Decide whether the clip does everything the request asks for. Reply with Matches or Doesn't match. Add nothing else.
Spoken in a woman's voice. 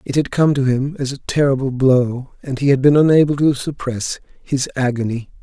Doesn't match